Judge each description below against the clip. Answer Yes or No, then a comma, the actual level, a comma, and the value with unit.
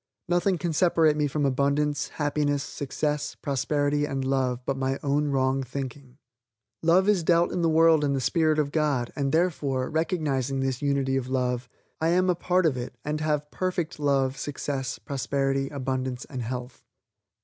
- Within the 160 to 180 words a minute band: Yes, average, 170 wpm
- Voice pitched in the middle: Yes, medium, 145 Hz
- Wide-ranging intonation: No, average, 2.8 semitones